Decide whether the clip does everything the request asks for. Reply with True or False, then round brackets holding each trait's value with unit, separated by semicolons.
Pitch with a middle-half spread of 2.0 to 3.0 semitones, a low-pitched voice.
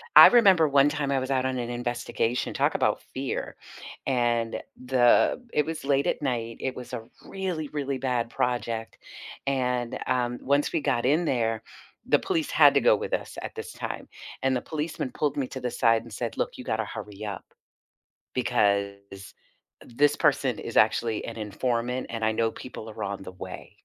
False (3.5 semitones; 125 Hz)